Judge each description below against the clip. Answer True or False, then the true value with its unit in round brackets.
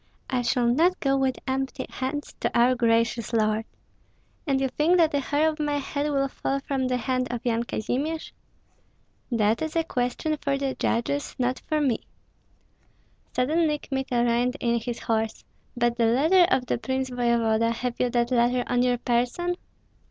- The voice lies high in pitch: True (255 Hz)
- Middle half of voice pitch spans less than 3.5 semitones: True (3.1 semitones)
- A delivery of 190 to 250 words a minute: False (175 wpm)